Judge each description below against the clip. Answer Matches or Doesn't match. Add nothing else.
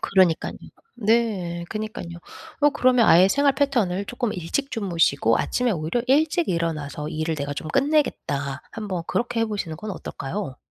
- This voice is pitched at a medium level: Doesn't match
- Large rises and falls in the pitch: Matches